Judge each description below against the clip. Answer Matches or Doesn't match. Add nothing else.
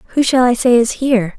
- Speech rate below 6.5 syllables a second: Doesn't match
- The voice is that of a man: Doesn't match